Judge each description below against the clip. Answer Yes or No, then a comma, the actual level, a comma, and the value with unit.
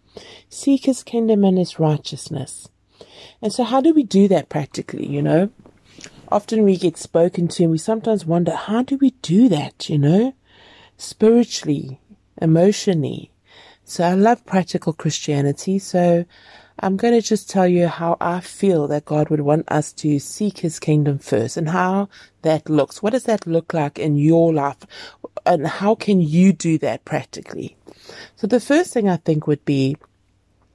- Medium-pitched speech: Yes, medium, 175 Hz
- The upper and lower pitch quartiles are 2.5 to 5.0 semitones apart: No, wide, 5.4 semitones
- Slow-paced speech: No, average, 170 wpm